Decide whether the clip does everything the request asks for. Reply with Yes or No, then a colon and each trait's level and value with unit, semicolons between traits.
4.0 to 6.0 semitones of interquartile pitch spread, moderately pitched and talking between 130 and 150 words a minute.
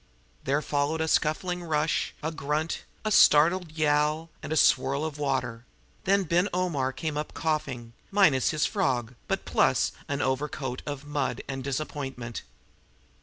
No: average, 3.1 semitones; medium, 150 Hz; average, 145 wpm